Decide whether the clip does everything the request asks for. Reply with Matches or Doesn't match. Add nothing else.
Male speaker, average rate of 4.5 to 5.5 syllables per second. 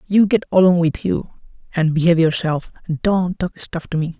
Matches